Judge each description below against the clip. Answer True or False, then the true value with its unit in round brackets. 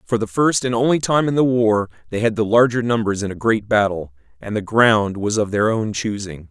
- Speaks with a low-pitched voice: True (110 Hz)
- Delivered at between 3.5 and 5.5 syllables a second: True (5.3 syllables/s)